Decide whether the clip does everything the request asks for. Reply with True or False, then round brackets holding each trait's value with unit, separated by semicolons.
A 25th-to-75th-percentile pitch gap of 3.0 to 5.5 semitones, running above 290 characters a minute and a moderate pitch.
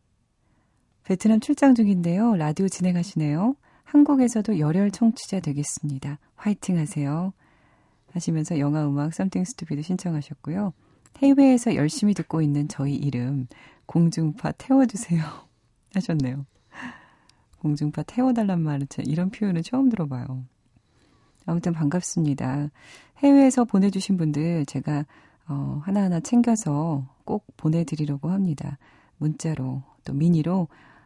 True (5.2 semitones; 315 characters per minute; 160 Hz)